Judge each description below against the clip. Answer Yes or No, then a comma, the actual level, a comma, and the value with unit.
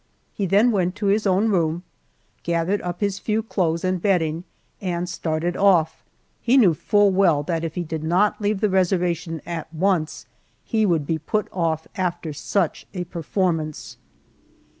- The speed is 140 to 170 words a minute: Yes, average, 160 wpm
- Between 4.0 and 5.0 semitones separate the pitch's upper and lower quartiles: No, average, 3.3 semitones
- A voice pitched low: No, medium, 180 Hz